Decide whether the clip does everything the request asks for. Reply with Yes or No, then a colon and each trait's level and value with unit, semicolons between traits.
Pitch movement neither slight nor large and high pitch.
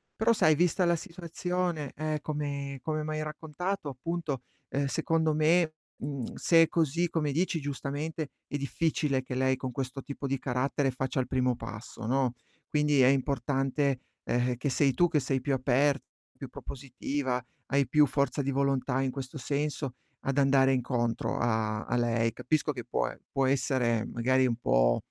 No: average, 3.1 semitones; medium, 140 Hz